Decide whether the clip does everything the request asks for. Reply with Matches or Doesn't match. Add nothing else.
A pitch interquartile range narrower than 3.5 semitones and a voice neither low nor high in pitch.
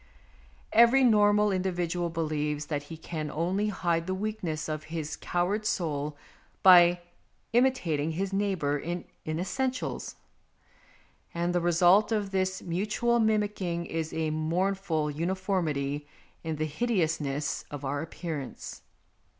Doesn't match